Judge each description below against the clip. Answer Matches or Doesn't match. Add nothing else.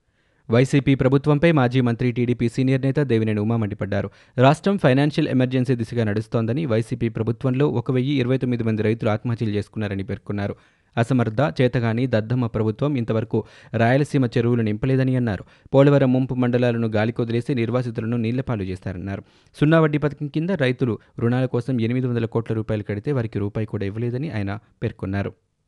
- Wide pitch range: Doesn't match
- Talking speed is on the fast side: Matches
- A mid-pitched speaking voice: Doesn't match